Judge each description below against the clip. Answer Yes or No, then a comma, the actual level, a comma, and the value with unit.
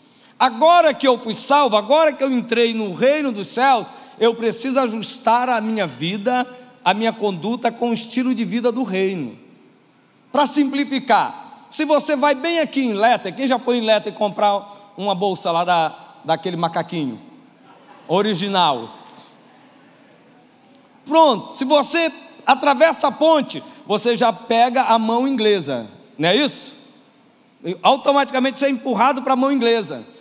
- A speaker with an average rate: Yes, average, 150 wpm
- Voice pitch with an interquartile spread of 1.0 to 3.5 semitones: No, average, 4.0 semitones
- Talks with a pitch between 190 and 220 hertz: No, very high, 250 Hz